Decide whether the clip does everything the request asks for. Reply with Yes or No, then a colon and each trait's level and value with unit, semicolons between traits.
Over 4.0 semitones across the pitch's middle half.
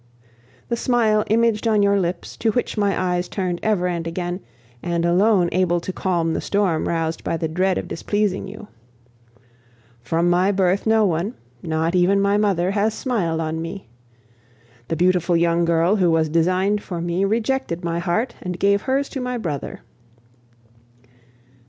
No: average, 3.5 semitones